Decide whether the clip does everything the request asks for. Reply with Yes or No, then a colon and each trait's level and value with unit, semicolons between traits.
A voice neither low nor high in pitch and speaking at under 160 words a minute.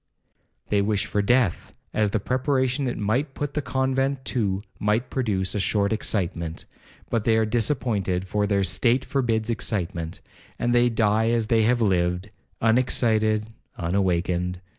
No: low, 110 Hz; average, 140 wpm